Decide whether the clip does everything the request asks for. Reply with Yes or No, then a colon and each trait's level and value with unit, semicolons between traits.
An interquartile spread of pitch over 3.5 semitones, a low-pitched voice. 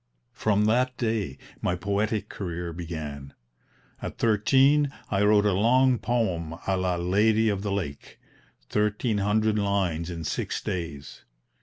Yes: average, 4.0 semitones; low, 100 Hz